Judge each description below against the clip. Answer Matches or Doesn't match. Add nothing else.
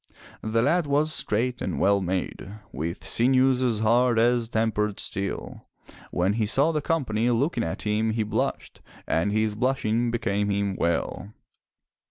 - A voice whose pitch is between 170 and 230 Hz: Doesn't match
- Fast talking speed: Doesn't match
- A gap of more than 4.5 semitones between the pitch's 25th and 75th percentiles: Doesn't match